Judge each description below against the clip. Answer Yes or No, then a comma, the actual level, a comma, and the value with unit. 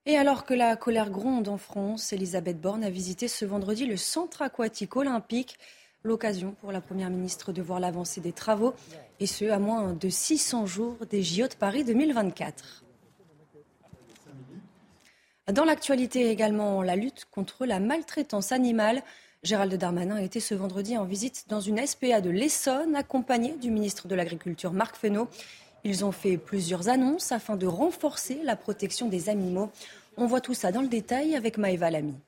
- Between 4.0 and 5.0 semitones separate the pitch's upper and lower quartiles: Yes, average, 4.5 semitones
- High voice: Yes, high, 215 Hz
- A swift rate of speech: No, average, 170 wpm